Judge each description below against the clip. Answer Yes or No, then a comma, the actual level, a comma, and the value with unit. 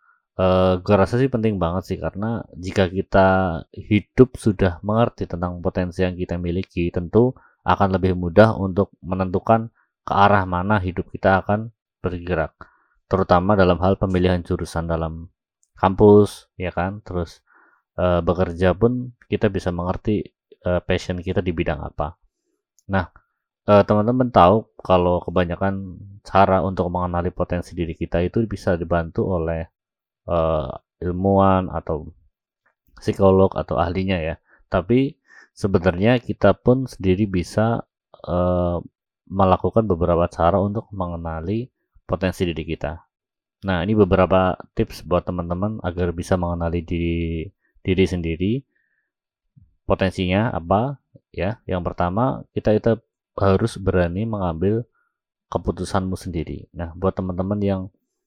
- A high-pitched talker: No, very low, 95 Hz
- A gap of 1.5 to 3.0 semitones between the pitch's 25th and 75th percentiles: Yes, narrow, 2.6 semitones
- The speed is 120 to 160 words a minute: Yes, average, 125 wpm